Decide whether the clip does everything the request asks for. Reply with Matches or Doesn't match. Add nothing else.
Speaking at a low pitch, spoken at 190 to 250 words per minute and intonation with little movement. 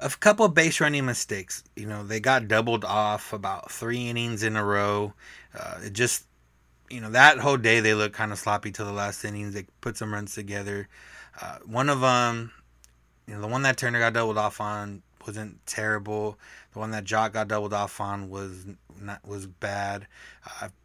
Matches